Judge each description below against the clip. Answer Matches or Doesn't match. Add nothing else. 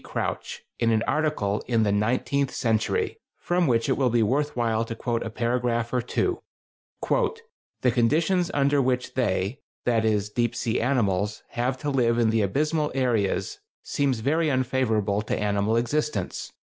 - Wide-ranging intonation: Doesn't match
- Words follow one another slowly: Doesn't match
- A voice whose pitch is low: Matches